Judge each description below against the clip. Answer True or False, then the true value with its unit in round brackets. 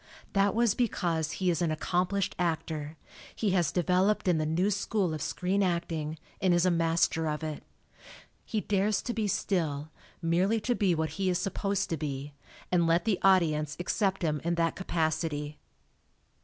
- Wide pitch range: False (3.6 semitones)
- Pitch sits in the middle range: True (175 Hz)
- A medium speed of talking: True (170 wpm)